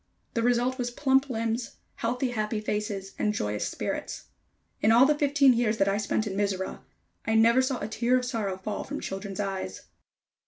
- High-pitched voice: Yes, high, 225 Hz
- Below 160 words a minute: No, average, 185 wpm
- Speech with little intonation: No, average, 3.6 semitones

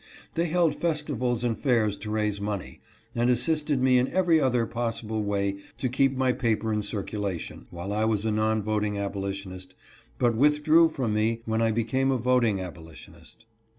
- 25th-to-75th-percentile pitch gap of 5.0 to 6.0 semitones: No, average, 3.8 semitones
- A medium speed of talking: Yes, average, 170 wpm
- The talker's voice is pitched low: Yes, low, 115 Hz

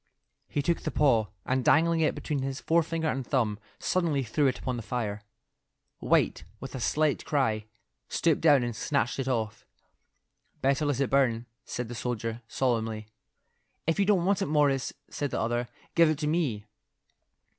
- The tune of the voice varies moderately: Yes, average, 4.6 semitones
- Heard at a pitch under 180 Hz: Yes, low, 135 Hz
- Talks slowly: No, average, 170 wpm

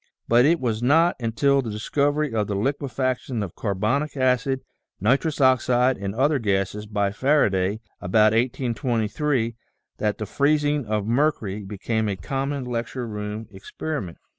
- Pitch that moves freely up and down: No, average, 4.6 semitones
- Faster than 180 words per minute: No, average, 140 wpm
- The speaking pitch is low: Yes, low, 120 Hz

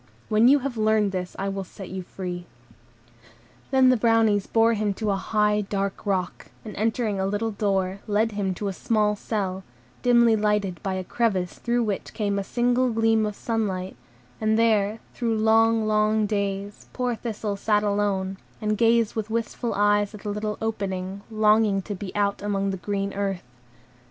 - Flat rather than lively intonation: Yes, narrow, 2.1 semitones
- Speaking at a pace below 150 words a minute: No, average, 175 wpm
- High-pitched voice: Yes, high, 210 Hz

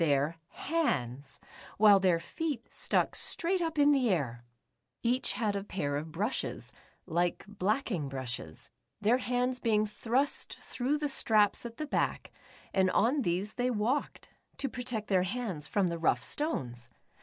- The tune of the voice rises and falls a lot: Yes, wide, 7.0 semitones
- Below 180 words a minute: Yes, average, 150 wpm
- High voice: Yes, high, 210 Hz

